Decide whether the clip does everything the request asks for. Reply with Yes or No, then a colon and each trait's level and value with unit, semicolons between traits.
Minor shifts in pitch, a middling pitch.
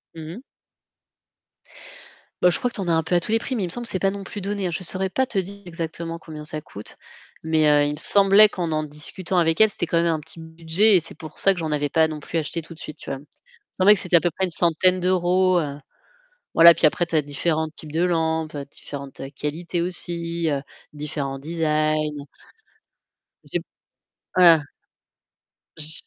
No: average, 3.0 semitones; medium, 165 Hz